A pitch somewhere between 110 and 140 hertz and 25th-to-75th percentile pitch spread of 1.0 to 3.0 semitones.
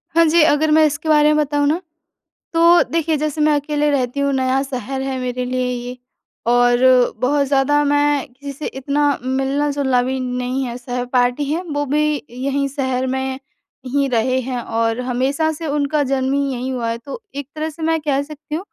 No: very high, 275 Hz; average, 2.7 semitones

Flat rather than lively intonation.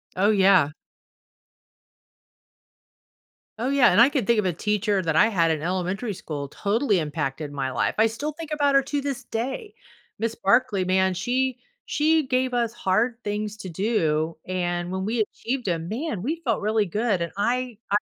No: wide, 5.6 semitones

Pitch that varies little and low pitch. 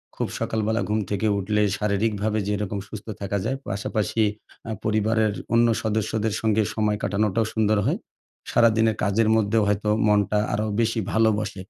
Yes: narrow, 1.2 semitones; low, 110 Hz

